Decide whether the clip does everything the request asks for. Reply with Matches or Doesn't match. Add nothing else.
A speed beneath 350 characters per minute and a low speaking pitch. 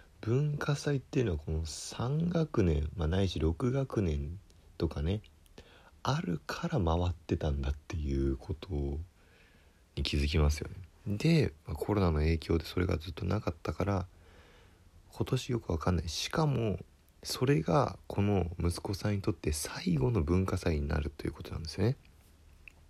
Matches